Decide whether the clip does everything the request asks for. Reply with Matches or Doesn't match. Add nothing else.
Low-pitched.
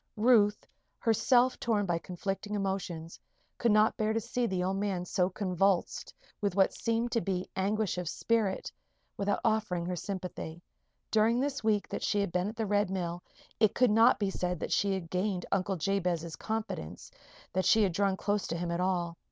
Doesn't match